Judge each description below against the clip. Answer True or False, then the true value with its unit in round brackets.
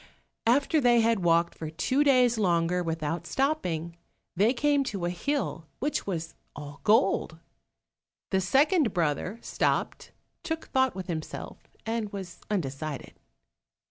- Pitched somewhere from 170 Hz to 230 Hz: True (190 Hz)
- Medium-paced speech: False (130 wpm)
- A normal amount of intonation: False (7.5 semitones)